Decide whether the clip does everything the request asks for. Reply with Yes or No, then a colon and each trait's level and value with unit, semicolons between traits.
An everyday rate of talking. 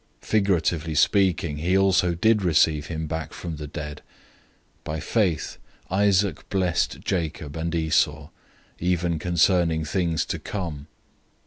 No: slow, 125 wpm